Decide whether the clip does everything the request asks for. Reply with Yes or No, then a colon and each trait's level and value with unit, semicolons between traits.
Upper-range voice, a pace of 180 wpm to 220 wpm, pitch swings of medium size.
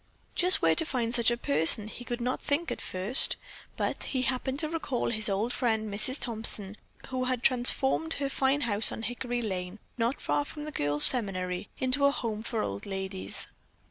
Yes: high, 240 Hz; average, 190 wpm; average, 4.2 semitones